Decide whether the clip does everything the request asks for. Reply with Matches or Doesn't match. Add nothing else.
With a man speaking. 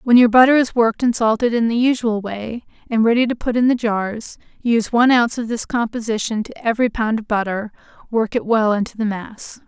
Doesn't match